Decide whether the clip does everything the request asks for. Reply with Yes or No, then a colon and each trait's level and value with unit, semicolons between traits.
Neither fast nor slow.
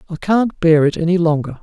No: fast, 220 wpm